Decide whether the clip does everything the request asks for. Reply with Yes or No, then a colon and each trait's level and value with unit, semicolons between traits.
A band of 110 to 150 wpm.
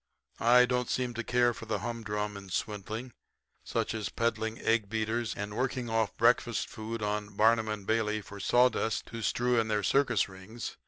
No: average, 175 wpm